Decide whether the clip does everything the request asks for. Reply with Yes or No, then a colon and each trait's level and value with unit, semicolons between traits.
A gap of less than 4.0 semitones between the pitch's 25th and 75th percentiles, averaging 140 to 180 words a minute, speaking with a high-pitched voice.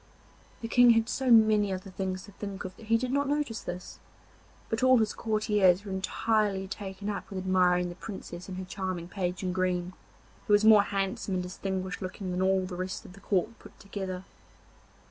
No: narrow, 2.6 semitones; average, 200 wpm; high, 195 Hz